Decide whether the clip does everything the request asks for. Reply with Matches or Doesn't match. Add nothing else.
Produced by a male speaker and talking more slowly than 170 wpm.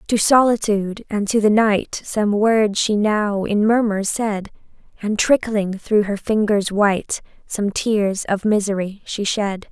Doesn't match